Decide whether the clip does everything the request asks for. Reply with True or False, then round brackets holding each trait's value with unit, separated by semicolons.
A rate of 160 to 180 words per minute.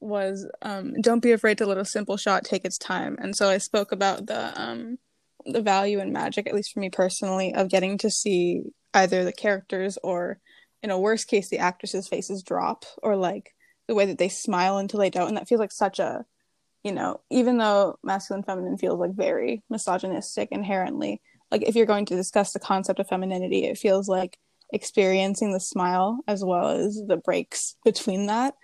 False (200 wpm)